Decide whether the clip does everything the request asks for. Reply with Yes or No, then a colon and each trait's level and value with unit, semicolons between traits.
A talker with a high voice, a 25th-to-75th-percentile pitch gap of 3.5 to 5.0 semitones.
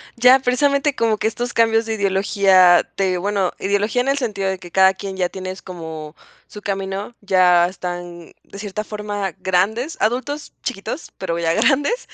Yes: high, 200 Hz; average, 3.8 semitones